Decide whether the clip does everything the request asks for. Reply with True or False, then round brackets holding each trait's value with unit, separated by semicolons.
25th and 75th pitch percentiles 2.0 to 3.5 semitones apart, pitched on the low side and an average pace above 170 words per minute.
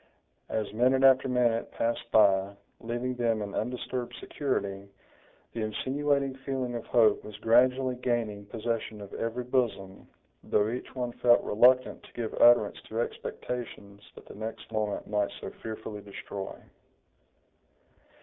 False (3.0 semitones; 115 Hz; 135 wpm)